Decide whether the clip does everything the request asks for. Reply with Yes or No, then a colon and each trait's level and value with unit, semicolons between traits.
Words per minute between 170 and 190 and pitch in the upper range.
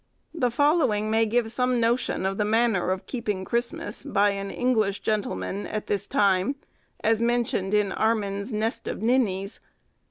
No: average, 155 wpm; high, 220 Hz